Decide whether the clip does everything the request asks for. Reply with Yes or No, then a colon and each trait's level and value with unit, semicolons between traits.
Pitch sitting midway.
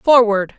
No: high, 225 Hz